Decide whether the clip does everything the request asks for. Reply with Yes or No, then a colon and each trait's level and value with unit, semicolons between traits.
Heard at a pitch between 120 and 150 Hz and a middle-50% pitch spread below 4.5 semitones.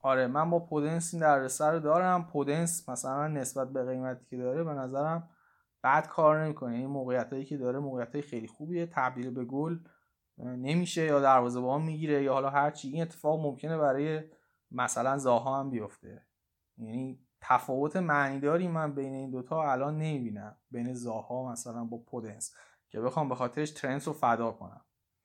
Yes: low, 135 Hz; average, 3.5 semitones